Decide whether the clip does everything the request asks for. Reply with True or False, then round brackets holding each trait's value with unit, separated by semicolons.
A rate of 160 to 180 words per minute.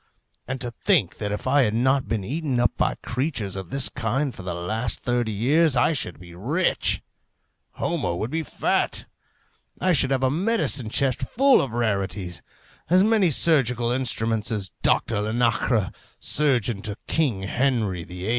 True (165 wpm)